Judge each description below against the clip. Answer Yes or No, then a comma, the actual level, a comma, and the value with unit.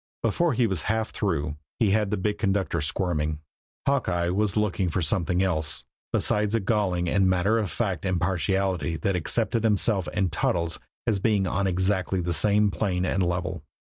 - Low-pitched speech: Yes, very low, 95 Hz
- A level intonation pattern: No, average, 3.1 semitones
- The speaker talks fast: No, average, 170 wpm